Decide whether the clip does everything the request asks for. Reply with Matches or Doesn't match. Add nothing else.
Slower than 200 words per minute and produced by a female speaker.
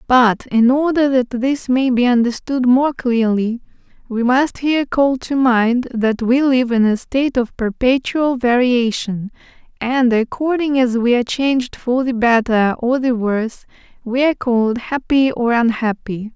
Matches